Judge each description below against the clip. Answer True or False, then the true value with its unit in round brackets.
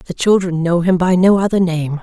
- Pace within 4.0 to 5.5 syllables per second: True (5.0 syllables/s)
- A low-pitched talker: False (180 Hz)